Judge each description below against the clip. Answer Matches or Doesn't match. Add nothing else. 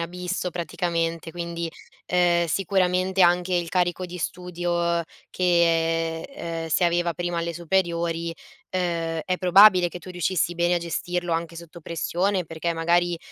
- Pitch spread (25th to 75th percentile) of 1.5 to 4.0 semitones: Doesn't match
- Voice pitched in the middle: Matches